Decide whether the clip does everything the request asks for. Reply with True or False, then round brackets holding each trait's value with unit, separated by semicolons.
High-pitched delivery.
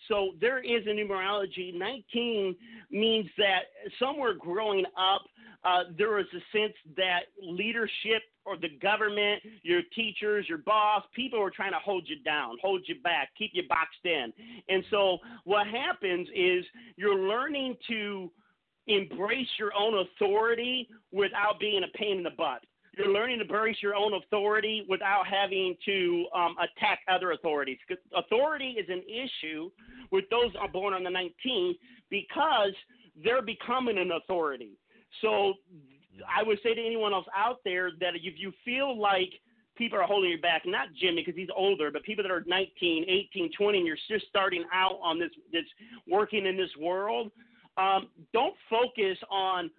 True (205 Hz)